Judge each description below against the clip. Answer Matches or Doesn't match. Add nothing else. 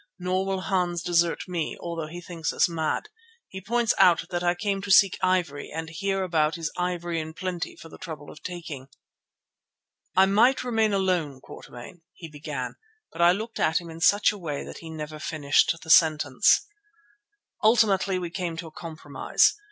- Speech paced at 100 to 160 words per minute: Doesn't match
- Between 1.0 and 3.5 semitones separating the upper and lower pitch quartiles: Matches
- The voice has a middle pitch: Matches